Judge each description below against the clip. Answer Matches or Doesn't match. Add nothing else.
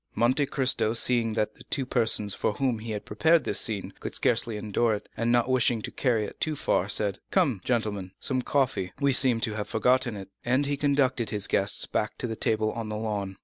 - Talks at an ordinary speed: Doesn't match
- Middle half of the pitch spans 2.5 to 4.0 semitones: Matches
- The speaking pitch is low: Matches